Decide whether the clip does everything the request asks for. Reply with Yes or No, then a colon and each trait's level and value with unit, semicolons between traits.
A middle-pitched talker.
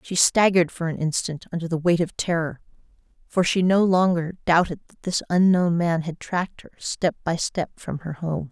Yes: medium, 170 Hz